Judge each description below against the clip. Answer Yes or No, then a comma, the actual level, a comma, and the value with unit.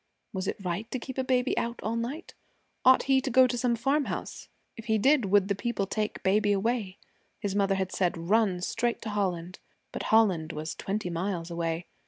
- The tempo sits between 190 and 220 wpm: Yes, average, 200 wpm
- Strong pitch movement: No, average, 4.3 semitones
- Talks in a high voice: Yes, high, 205 Hz